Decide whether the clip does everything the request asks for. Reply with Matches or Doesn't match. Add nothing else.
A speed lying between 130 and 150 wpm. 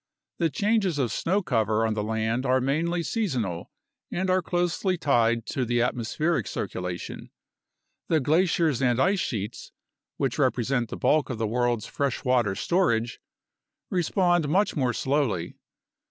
Matches